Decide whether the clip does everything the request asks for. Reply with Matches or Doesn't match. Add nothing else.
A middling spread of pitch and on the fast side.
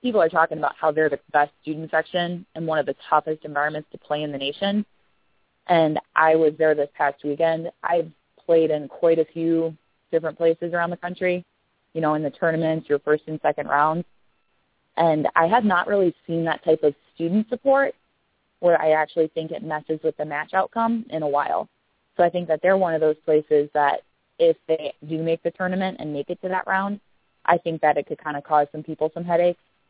Doesn't match